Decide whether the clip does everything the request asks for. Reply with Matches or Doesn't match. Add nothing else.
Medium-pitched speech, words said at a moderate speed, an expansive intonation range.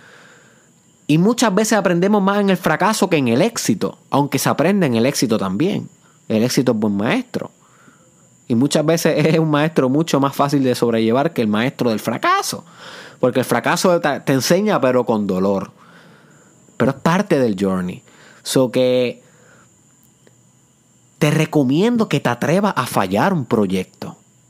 Matches